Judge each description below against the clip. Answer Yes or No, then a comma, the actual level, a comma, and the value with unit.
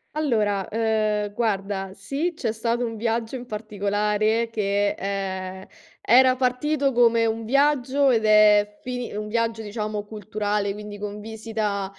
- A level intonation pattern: Yes, narrow, 2.3 semitones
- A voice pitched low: No, high, 215 Hz